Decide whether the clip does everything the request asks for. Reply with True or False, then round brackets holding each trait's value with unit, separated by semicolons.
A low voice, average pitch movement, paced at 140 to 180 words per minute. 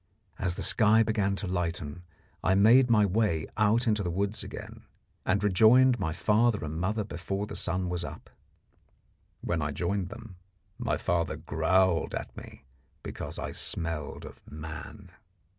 True (95 Hz; 4.1 semitones; 155 wpm)